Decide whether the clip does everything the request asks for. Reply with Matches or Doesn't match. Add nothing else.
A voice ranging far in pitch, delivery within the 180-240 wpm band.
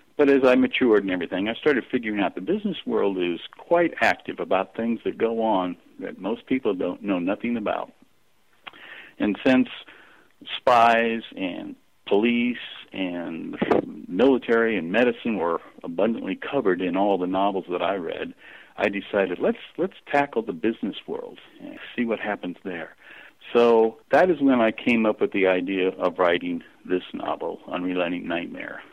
Doesn't match